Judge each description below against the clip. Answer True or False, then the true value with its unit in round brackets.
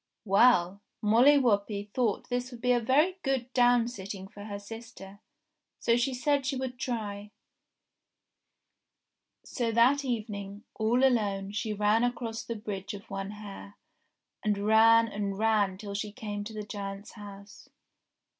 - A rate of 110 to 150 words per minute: True (145 wpm)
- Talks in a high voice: True (215 Hz)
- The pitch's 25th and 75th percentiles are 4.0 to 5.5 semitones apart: False (3.2 semitones)